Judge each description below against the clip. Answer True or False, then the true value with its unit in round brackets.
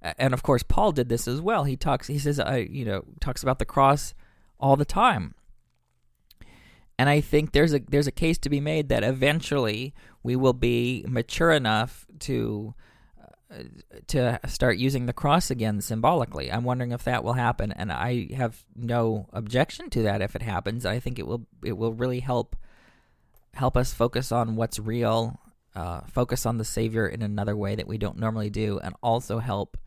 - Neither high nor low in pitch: False (120 Hz)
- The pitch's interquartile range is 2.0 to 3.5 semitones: True (3.2 semitones)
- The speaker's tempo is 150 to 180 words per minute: False (190 wpm)